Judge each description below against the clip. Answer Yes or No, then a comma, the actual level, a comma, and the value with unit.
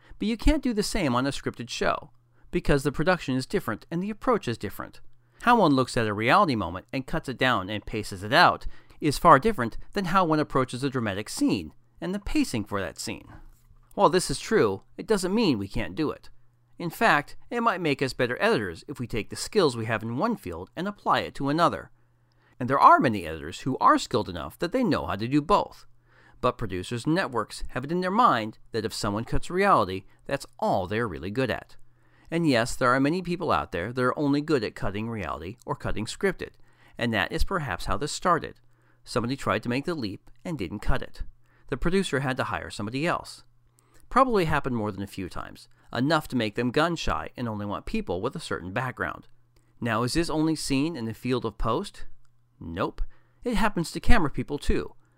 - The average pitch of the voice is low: Yes, low, 125 Hz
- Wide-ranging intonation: Yes, wide, 5.7 semitones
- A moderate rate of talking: No, fast, 220 wpm